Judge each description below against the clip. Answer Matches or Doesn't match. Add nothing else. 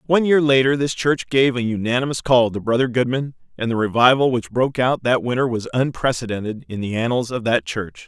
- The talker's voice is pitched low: Matches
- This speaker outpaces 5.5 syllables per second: Matches